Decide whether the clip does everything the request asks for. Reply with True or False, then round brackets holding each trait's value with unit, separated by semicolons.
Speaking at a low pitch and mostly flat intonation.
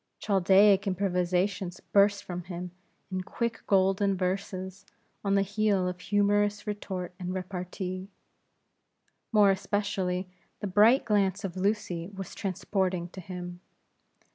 False (190 Hz; 1.9 semitones)